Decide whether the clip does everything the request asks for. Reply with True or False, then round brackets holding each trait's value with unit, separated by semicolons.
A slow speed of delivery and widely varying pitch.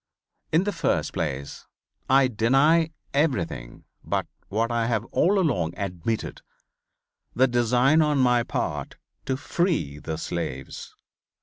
True (120 wpm; 7.2 semitones)